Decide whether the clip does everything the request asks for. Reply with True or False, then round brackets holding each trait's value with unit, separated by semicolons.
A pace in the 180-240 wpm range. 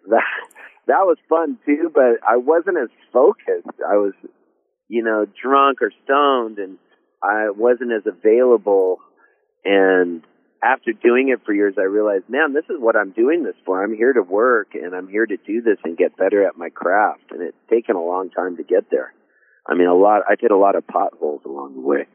True (205 wpm)